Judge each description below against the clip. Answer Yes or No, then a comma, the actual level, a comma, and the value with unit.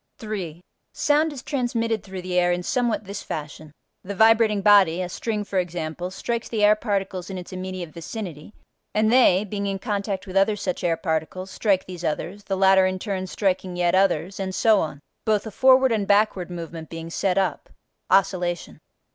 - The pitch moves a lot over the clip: No, average, 3.0 semitones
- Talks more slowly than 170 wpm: No, average, 185 wpm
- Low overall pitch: No, high, 190 Hz